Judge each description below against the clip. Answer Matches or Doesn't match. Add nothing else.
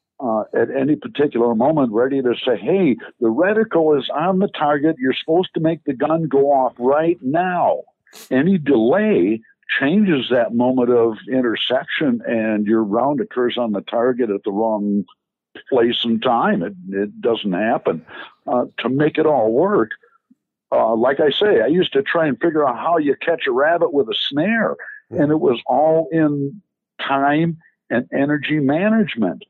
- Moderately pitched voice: Matches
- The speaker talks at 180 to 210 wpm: Doesn't match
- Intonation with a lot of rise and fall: Matches